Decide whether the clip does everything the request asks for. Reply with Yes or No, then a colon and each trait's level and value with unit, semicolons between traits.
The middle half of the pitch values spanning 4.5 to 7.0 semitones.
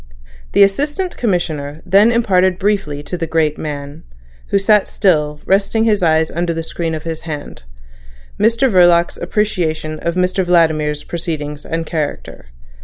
No: average, 4.1 semitones